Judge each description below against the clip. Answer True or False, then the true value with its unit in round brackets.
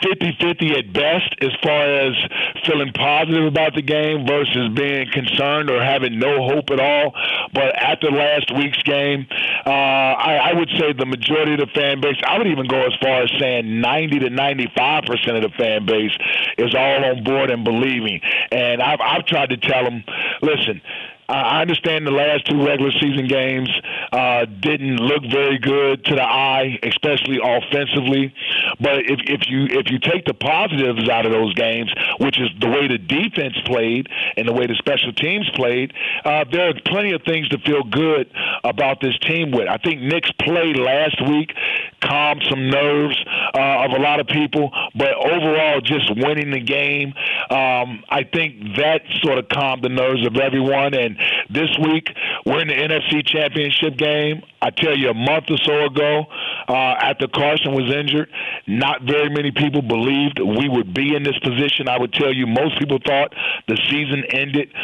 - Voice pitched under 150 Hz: True (140 Hz)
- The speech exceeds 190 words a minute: False (185 wpm)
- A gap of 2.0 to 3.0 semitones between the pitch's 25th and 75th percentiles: True (2.5 semitones)